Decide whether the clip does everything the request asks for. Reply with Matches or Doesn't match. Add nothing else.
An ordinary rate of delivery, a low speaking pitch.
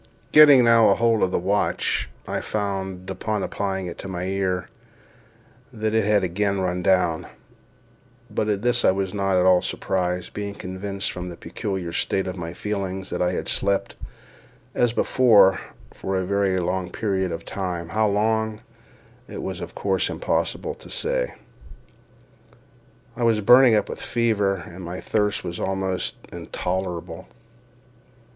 Matches